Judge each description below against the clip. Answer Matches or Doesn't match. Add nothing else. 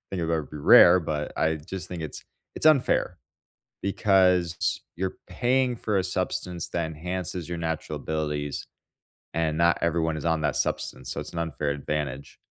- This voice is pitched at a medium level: Doesn't match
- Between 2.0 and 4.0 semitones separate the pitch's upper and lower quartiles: Matches